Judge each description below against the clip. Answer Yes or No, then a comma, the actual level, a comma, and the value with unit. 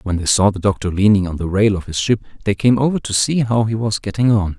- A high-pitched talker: No, low, 105 Hz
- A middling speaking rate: No, fast, 290 wpm